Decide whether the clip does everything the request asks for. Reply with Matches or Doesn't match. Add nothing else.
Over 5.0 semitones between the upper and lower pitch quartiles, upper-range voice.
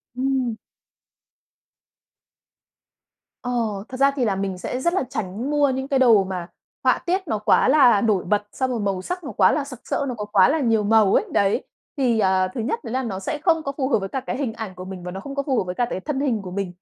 Matches